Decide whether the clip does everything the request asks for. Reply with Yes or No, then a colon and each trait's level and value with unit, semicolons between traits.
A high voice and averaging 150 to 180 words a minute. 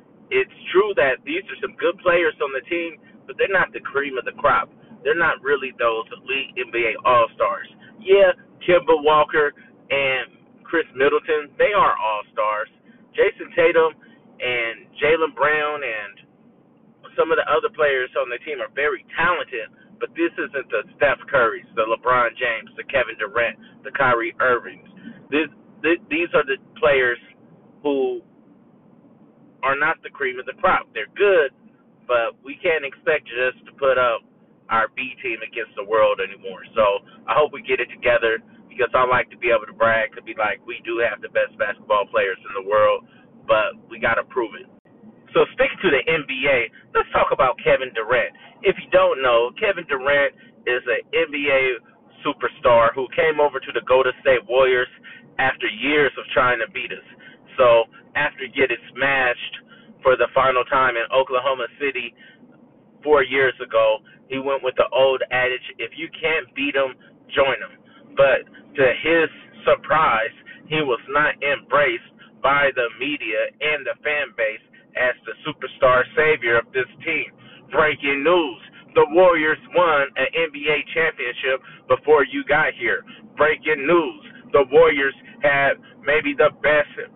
Yes: high, 205 Hz; average, 160 wpm